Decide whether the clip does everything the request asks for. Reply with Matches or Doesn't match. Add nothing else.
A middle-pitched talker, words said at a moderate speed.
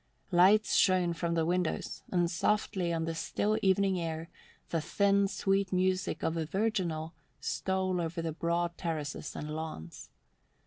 Matches